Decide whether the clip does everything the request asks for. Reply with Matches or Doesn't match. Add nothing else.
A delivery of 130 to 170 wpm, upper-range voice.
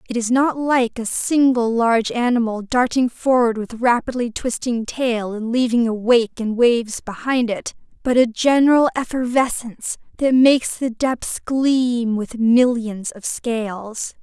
Matches